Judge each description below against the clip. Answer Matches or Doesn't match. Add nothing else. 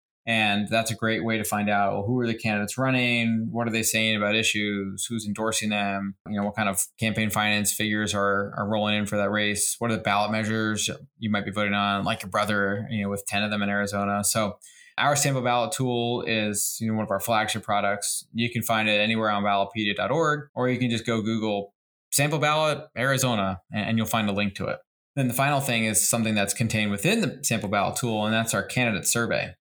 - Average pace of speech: Doesn't match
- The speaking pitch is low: Matches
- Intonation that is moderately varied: Doesn't match